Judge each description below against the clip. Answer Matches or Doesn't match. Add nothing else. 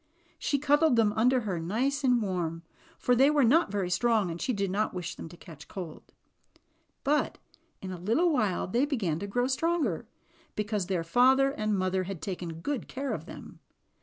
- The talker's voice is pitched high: Matches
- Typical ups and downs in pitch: Doesn't match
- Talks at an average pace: Matches